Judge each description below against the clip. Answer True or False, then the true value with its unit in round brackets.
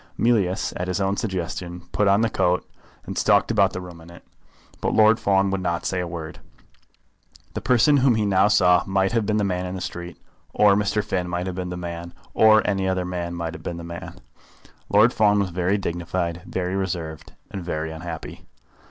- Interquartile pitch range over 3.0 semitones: False (2.6 semitones)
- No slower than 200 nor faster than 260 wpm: True (205 wpm)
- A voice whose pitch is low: True (90 Hz)